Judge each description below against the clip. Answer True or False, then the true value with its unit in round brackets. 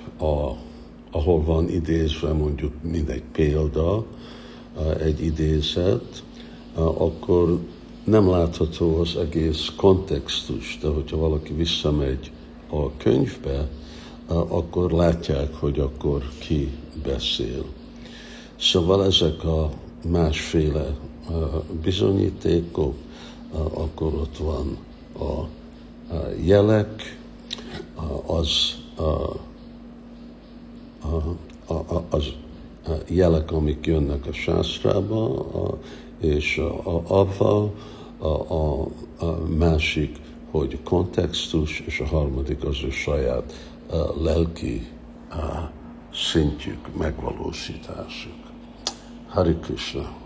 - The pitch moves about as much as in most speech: False (1.4 semitones)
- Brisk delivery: False (90 wpm)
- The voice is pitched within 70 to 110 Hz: True (80 Hz)